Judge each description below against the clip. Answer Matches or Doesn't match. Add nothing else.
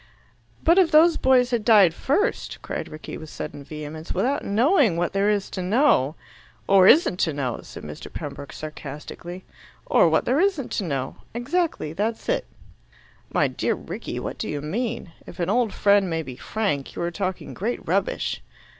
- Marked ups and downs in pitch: Matches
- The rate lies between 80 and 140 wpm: Doesn't match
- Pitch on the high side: Matches